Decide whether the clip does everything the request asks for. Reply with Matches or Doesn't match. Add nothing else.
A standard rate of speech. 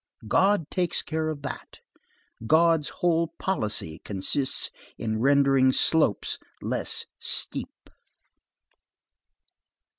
Doesn't match